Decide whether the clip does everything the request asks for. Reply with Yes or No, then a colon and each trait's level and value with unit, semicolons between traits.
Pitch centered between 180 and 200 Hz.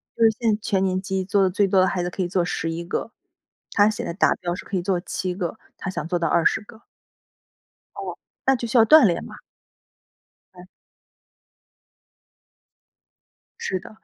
Yes: high, 190 Hz